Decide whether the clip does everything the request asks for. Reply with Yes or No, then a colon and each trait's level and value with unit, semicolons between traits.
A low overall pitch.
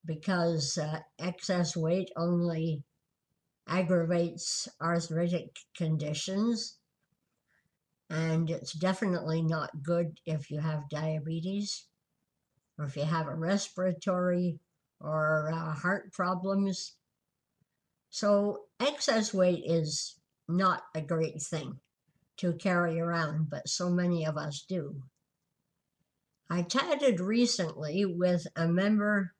No: medium, 170 Hz